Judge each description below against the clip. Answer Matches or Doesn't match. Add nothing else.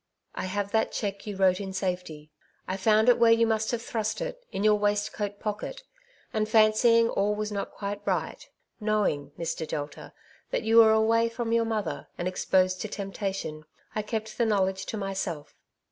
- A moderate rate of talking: Matches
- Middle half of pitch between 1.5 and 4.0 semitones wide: Matches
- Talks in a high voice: Matches